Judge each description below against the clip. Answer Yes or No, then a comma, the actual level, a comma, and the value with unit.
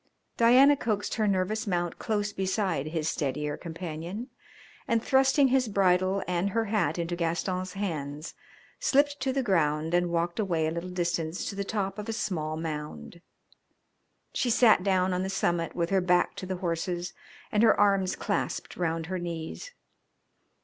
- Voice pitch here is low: No, medium, 185 Hz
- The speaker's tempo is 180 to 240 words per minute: No, average, 165 wpm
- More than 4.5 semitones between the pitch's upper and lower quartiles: No, average, 3.7 semitones